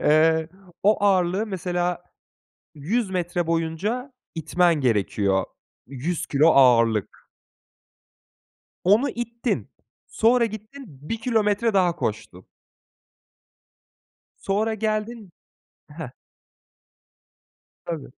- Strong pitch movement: Yes, wide, 5.9 semitones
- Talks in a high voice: No, medium, 180 Hz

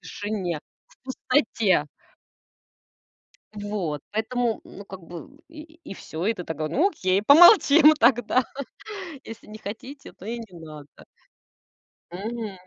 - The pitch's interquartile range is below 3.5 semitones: No, wide, 5.5 semitones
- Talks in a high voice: Yes, high, 215 Hz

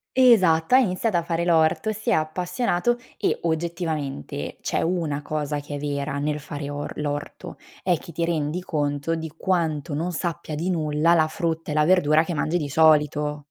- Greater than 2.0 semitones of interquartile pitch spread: Yes, average, 2.7 semitones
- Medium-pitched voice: Yes, medium, 160 Hz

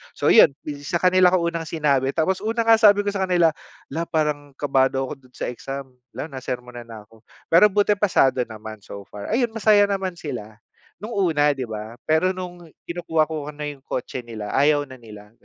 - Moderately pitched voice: Yes, medium, 150 Hz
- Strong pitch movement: Yes, wide, 6.1 semitones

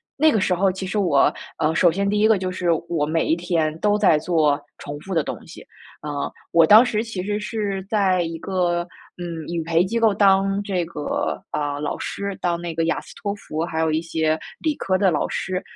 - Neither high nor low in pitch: Yes, medium, 180 Hz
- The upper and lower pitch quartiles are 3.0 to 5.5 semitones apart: Yes, average, 3.6 semitones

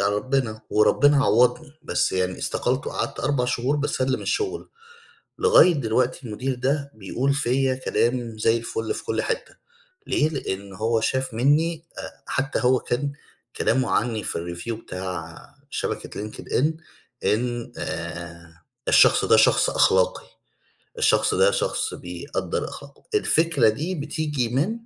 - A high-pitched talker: No, low, 125 Hz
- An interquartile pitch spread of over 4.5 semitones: Yes, average, 4.9 semitones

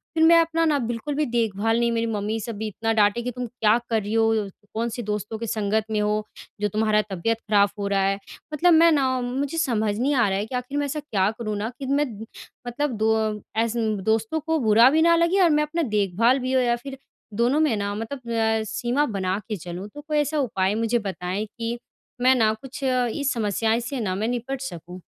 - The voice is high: Yes, high, 230 Hz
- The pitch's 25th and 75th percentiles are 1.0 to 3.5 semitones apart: No, average, 4.1 semitones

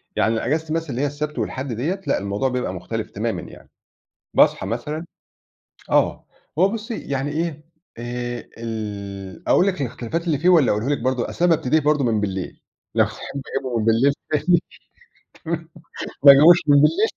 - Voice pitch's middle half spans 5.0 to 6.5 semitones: Yes, average, 5.3 semitones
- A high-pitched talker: No, medium, 140 Hz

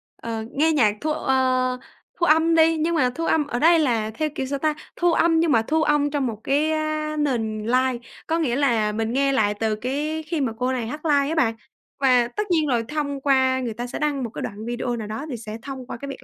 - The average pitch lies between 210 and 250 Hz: No, very high, 270 Hz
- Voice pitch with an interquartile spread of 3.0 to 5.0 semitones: Yes, average, 4.4 semitones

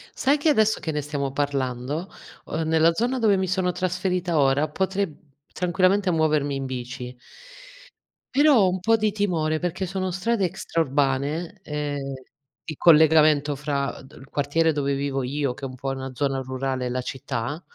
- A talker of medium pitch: Yes, medium, 155 Hz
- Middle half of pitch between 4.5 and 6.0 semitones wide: Yes, average, 5.1 semitones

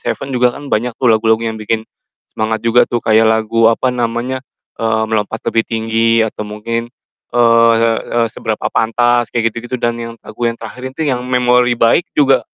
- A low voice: Yes, low, 115 Hz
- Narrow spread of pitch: Yes, narrow, 1.5 semitones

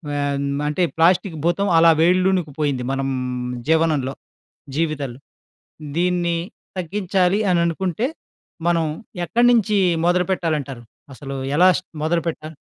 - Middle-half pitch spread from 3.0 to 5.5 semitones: Yes, average, 3.5 semitones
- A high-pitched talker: No, medium, 170 Hz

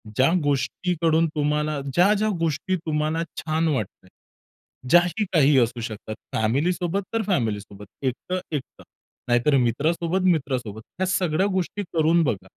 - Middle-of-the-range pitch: Yes, medium, 155 Hz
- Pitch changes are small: No, wide, 5.5 semitones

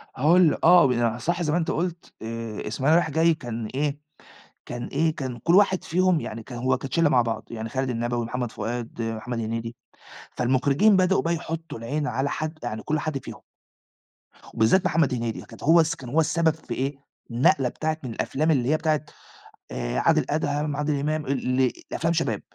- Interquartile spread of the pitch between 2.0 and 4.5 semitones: No, average, 5.0 semitones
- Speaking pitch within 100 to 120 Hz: No, medium, 140 Hz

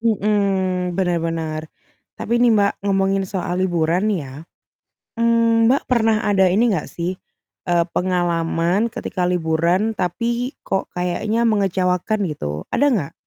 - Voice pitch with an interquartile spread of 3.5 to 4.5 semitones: Yes, average, 3.9 semitones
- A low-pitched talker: No, high, 190 Hz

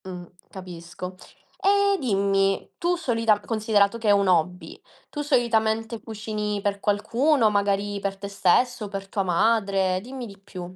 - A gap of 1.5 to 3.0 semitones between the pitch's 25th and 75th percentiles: Yes, average, 2.7 semitones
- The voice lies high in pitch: Yes, high, 205 Hz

